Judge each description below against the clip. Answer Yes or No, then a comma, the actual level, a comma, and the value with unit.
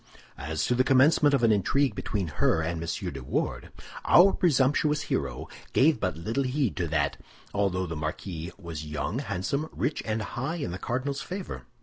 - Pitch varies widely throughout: Yes, wide, 8.9 semitones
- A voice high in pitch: No, low, 110 Hz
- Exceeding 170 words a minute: Yes, average, 180 wpm